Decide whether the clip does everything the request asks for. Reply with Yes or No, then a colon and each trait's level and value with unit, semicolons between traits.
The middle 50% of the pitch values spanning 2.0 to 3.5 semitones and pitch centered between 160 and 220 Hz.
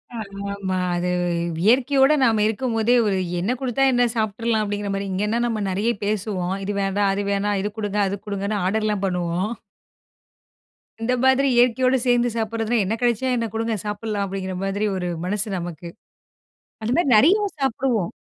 Yes: average, 3.2 semitones; high, 215 Hz